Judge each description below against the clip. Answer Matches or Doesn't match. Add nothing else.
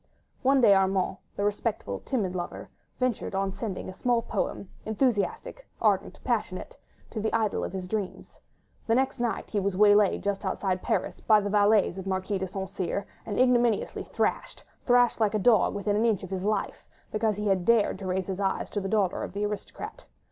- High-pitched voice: Matches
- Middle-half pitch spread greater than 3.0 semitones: Doesn't match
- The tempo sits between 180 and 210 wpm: Matches